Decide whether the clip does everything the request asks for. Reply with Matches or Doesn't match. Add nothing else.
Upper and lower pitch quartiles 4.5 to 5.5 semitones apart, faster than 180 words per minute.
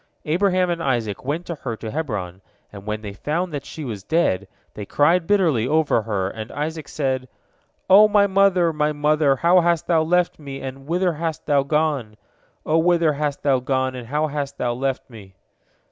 Matches